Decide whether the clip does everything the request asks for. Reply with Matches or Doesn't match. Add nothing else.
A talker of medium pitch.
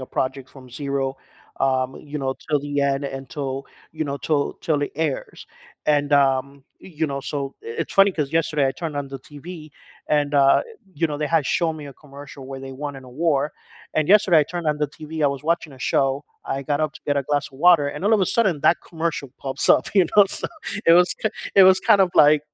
Matches